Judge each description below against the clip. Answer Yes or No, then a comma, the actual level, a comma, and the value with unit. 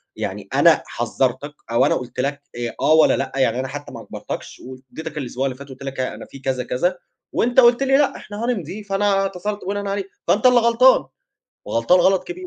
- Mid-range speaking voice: Yes, medium, 175 Hz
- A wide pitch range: Yes, wide, 7.8 semitones